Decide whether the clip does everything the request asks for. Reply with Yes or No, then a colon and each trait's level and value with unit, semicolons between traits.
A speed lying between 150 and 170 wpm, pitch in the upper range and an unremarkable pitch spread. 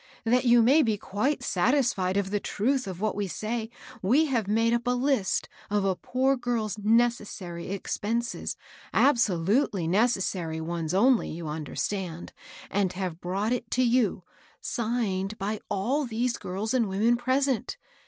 Yes: average, 160 wpm; high, 215 Hz; average, 4.3 semitones